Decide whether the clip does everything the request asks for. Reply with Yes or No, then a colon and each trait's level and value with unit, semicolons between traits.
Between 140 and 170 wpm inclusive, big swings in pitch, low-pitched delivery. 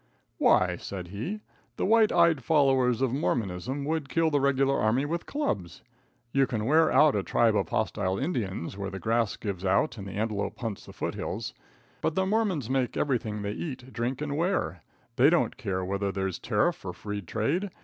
No: average, 185 wpm; wide, 6.7 semitones; low, 120 Hz